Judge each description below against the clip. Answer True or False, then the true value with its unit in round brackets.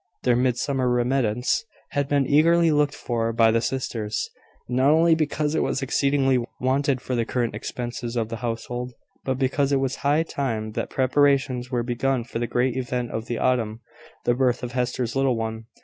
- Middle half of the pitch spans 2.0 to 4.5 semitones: True (2.5 semitones)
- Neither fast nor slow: True (180 wpm)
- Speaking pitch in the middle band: False (125 Hz)